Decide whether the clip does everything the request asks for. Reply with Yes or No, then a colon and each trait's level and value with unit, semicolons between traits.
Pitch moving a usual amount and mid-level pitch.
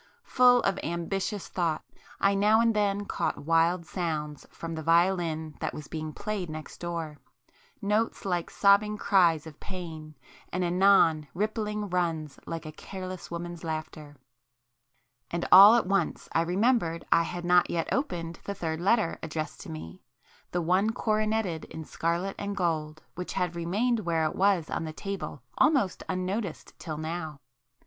Yes: average, 3.9 semitones; medium, 175 Hz